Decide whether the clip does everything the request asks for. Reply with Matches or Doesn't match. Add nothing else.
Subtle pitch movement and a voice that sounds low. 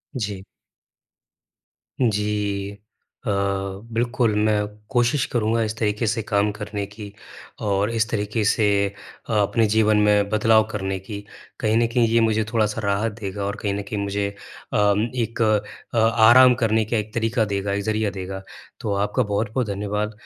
Matches